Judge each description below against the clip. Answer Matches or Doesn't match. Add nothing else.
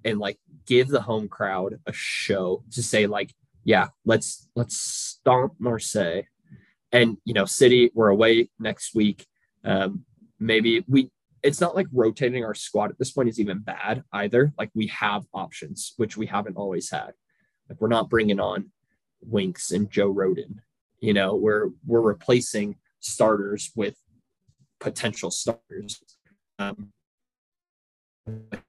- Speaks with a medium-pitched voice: Doesn't match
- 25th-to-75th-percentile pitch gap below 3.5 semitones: Matches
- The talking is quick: Doesn't match